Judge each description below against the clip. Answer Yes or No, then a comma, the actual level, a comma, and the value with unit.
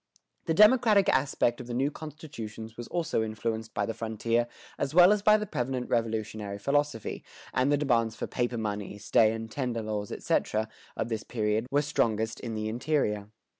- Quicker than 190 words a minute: No, average, 175 wpm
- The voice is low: Yes, low, 115 Hz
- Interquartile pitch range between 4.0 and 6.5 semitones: Yes, average, 4.6 semitones